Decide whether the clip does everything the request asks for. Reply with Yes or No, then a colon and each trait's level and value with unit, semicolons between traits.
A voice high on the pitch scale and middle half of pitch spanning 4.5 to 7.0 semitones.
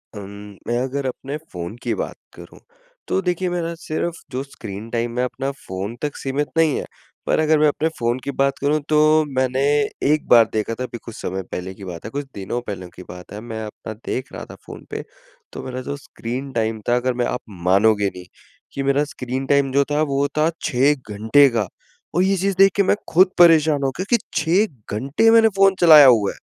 No: low, 135 Hz; average, 5.2 semitones